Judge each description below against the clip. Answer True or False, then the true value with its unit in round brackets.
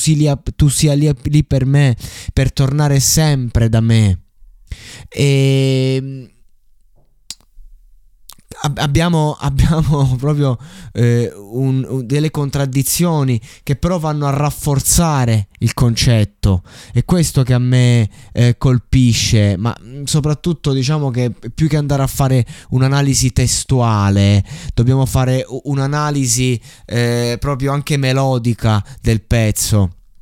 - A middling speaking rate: False (105 wpm)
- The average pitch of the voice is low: True (130 Hz)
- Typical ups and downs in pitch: True (3.3 semitones)